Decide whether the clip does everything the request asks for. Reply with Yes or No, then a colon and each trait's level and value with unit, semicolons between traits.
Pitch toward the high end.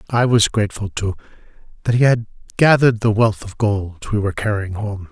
No: low, 105 Hz